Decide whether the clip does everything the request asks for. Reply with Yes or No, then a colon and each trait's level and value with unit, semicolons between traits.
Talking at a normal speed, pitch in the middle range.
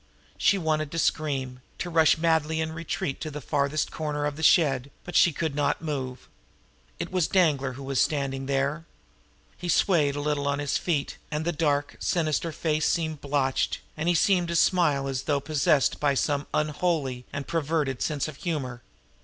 Yes: average, 185 wpm; medium, 150 Hz